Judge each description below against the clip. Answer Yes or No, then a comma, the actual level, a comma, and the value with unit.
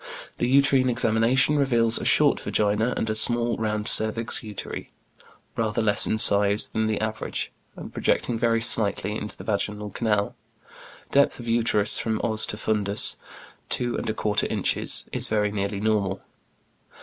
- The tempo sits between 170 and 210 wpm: No, average, 155 wpm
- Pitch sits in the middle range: No, low, 110 Hz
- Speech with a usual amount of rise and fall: No, narrow, 2.0 semitones